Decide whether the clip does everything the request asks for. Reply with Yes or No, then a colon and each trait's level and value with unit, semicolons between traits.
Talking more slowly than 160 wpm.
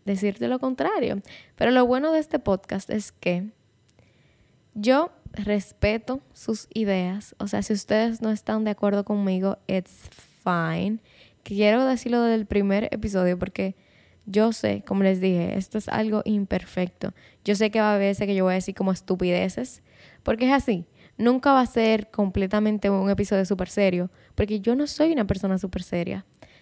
No: average, 170 wpm